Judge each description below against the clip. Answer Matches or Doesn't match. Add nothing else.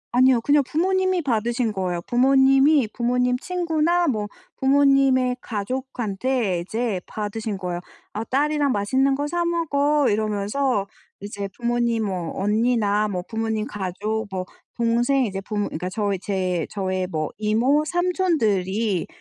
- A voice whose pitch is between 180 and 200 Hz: Doesn't match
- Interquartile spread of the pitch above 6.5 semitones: Doesn't match